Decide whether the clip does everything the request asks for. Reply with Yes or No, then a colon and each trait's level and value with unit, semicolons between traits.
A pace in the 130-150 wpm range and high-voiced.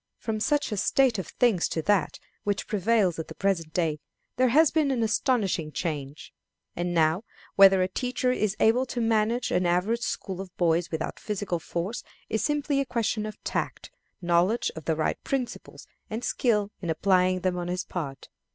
No: average, 180 wpm; high, 195 Hz